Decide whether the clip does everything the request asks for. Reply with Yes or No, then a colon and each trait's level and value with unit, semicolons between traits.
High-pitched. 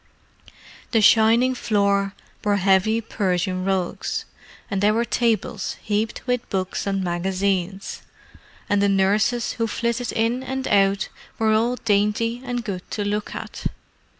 Yes: high, 210 Hz